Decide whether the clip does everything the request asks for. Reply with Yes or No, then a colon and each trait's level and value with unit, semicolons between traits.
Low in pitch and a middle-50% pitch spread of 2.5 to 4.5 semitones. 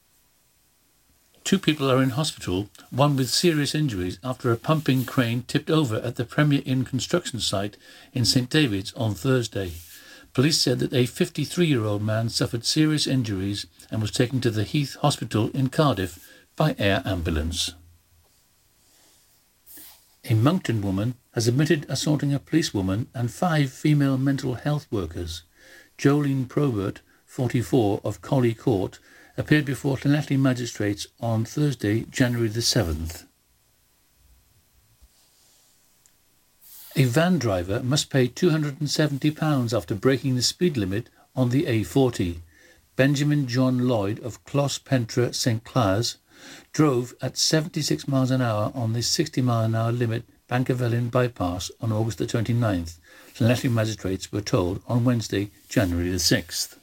No: low, 125 Hz; average, 5.3 semitones